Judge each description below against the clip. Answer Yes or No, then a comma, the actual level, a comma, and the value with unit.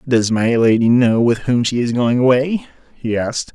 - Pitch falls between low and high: No, low, 120 Hz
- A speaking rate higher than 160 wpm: Yes, fast, 205 wpm